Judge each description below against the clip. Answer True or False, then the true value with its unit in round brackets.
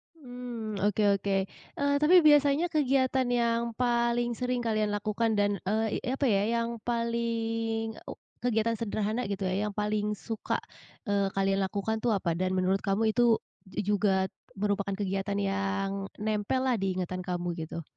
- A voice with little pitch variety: False (3.2 semitones)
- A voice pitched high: True (215 Hz)